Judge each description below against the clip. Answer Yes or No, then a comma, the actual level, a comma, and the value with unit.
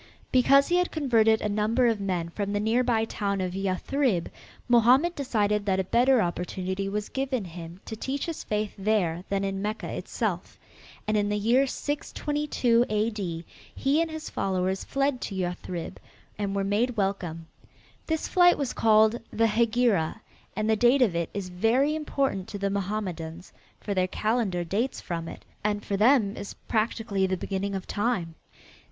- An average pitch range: Yes, average, 4.2 semitones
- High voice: Yes, high, 210 Hz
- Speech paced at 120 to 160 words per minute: No, average, 170 wpm